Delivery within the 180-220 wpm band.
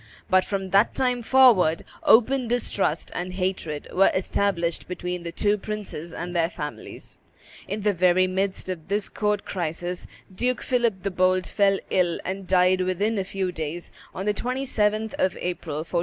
No: average, 165 wpm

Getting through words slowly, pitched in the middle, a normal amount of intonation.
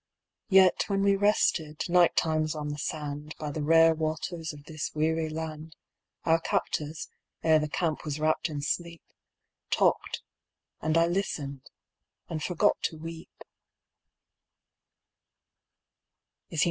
No: slow, 120 wpm; medium, 160 Hz; narrow, 1.6 semitones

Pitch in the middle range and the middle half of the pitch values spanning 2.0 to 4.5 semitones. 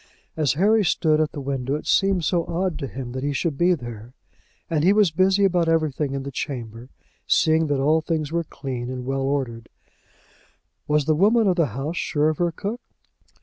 Yes: medium, 155 Hz; average, 4.2 semitones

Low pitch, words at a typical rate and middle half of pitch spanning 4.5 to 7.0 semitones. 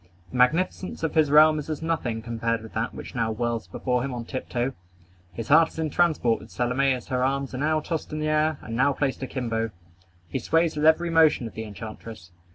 No: low, 130 Hz; fast, 220 wpm; average, 5.0 semitones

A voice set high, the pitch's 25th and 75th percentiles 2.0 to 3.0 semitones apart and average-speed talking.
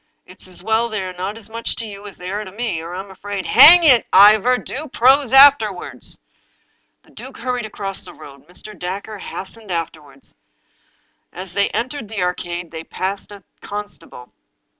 No: high, 200 Hz; average, 3.9 semitones; average, 195 wpm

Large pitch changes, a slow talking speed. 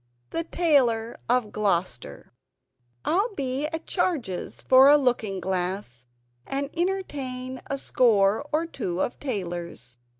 Yes: wide, 7.2 semitones; slow, 120 wpm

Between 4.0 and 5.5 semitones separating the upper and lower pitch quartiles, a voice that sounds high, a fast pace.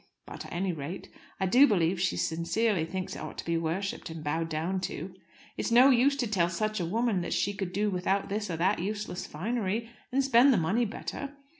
Yes: average, 5.0 semitones; high, 195 Hz; fast, 215 wpm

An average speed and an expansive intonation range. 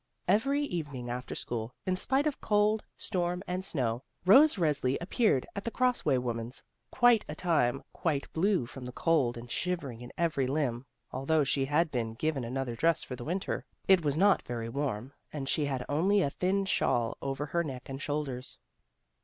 Yes: average, 185 wpm; wide, 6.3 semitones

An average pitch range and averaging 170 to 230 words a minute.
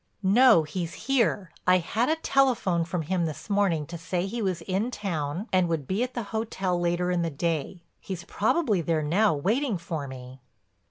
Yes: average, 4.3 semitones; average, 180 wpm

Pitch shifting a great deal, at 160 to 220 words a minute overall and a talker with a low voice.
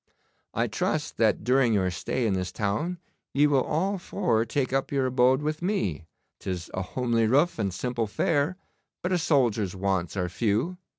Yes: wide, 6.7 semitones; average, 175 wpm; low, 125 Hz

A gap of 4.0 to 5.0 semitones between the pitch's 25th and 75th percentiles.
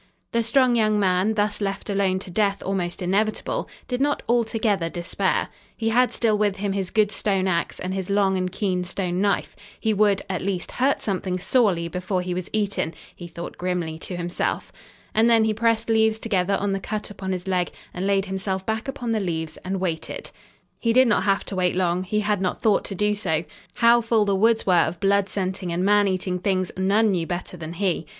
No: average, 2.8 semitones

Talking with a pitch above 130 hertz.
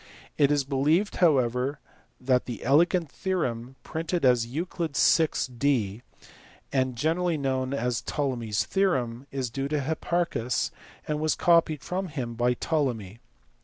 Yes: medium, 140 Hz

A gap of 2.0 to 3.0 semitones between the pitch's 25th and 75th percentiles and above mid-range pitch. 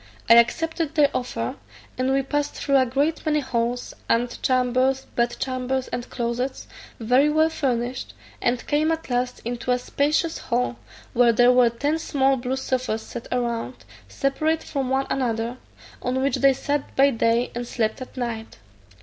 Yes: narrow, 2.4 semitones; very high, 255 Hz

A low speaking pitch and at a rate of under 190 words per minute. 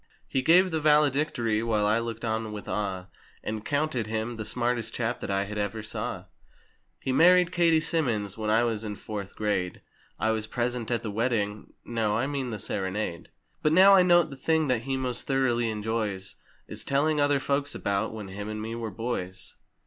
No: low, 115 Hz; average, 195 wpm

